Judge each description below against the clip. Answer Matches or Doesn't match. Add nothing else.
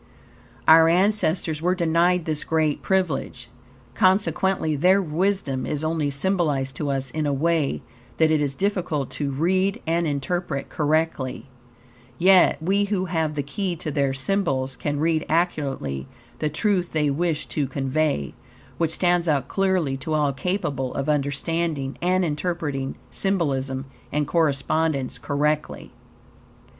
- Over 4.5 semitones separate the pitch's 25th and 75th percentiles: Doesn't match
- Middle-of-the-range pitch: Matches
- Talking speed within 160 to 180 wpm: Doesn't match